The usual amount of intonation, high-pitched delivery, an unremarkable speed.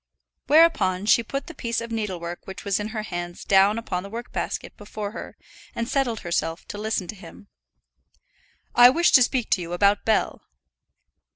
Yes: average, 3.6 semitones; high, 210 Hz; average, 180 wpm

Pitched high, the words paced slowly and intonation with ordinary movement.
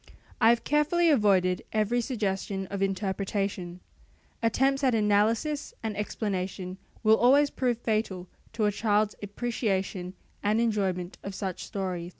Yes: high, 210 Hz; slow, 130 wpm; average, 3.4 semitones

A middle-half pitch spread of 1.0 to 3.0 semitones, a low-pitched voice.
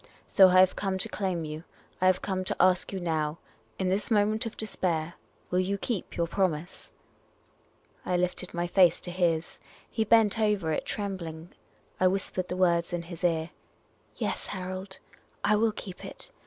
No: narrow, 2.4 semitones; medium, 185 Hz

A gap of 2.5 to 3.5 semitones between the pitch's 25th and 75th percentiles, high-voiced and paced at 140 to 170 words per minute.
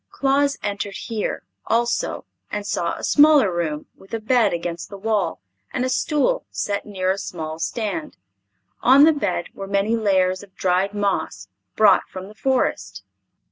No: average, 4.2 semitones; high, 200 Hz; average, 160 wpm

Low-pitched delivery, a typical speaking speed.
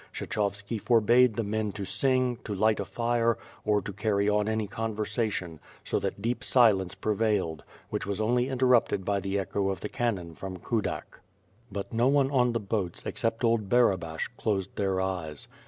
Yes: low, 105 Hz; average, 170 wpm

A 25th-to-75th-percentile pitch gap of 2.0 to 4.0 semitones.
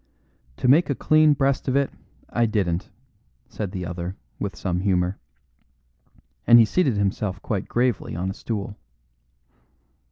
No: wide, 5.4 semitones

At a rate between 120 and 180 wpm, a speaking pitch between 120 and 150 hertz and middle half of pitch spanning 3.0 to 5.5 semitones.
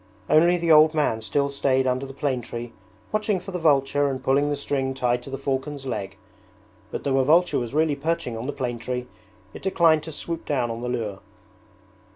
No: fast, 205 wpm; low, 135 Hz; average, 3.7 semitones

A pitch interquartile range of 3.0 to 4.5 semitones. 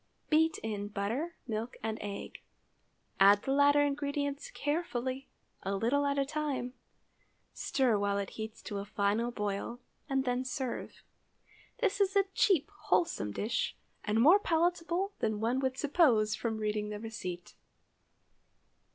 No: wide, 5.5 semitones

